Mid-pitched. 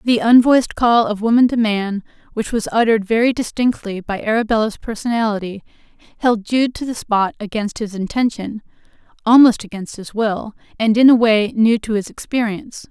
No: high, 220 Hz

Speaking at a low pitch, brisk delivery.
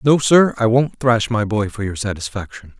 Yes: low, 115 Hz; fast, 215 wpm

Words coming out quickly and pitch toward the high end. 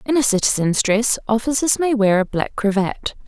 No: average, 185 wpm; high, 225 Hz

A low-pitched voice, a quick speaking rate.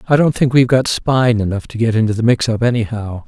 Yes: low, 115 Hz; fast, 255 wpm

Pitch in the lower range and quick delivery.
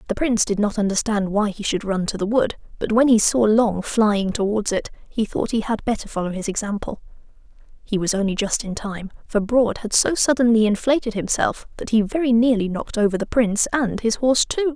No: high, 220 Hz; fast, 215 wpm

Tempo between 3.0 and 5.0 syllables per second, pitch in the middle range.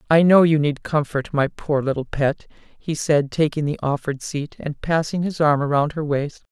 Yes: 4.6 syllables/s; medium, 150 Hz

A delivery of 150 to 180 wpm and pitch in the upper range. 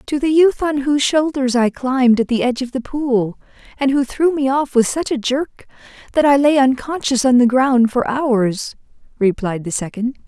No: fast, 205 wpm; very high, 260 Hz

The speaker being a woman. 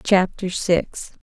Yes: female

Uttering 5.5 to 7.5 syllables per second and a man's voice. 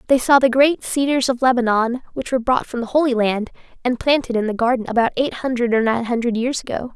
No: 6.1 syllables/s; female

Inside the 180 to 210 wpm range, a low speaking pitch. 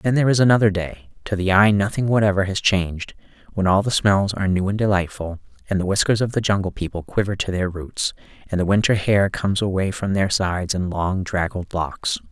Yes: fast, 205 wpm; low, 100 Hz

